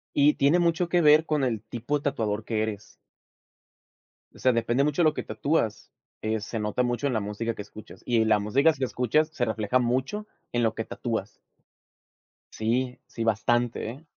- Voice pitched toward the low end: Yes, low, 120 Hz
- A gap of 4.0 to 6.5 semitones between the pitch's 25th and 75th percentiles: Yes, average, 4.5 semitones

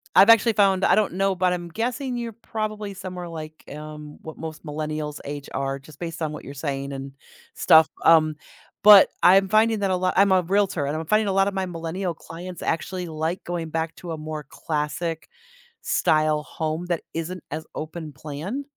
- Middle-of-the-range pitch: Yes, medium, 165 Hz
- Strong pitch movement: No, average, 3.9 semitones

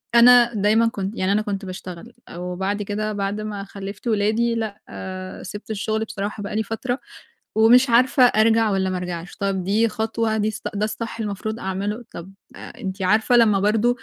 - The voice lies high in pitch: Yes, high, 210 Hz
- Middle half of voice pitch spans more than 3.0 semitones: No, narrow, 2.4 semitones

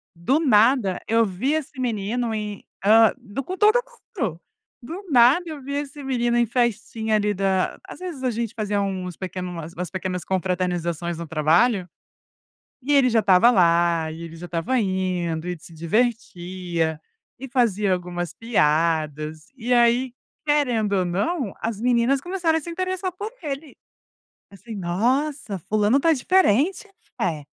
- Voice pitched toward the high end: Yes, high, 215 Hz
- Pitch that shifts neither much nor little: No, wide, 6.5 semitones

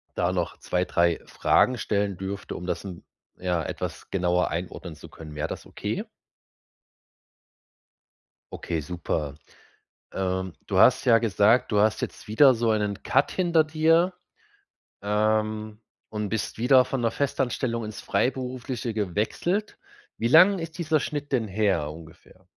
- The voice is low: Yes, low, 110 Hz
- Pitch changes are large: Yes, wide, 5.9 semitones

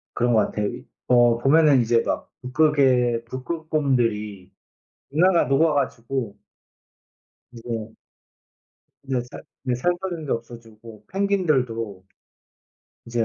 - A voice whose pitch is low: Yes, low, 125 Hz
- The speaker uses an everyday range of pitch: Yes, average, 4.4 semitones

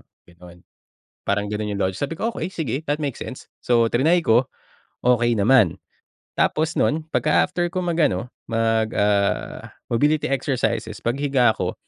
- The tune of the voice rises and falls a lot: Yes, wide, 5.9 semitones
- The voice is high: No, low, 120 Hz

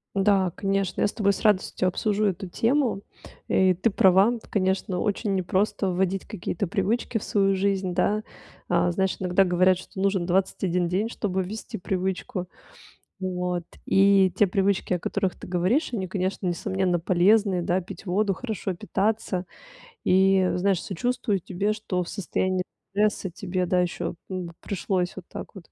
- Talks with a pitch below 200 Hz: Yes, high, 190 Hz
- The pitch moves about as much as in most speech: No, narrow, 1.8 semitones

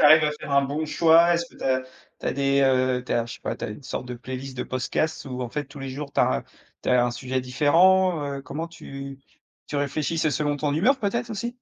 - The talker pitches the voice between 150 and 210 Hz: No, medium, 140 Hz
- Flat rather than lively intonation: No, average, 3.7 semitones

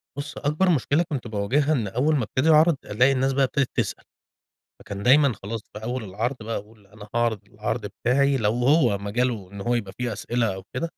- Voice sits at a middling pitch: No, low, 120 Hz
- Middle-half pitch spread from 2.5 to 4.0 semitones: No, average, 4.7 semitones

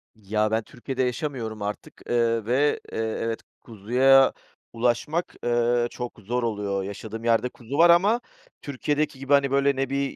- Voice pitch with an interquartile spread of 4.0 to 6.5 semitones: No, average, 3.6 semitones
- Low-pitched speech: Yes, low, 120 Hz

